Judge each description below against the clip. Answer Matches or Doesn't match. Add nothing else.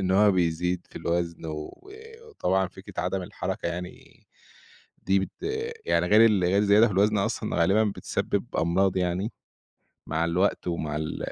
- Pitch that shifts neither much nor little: Matches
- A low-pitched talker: Matches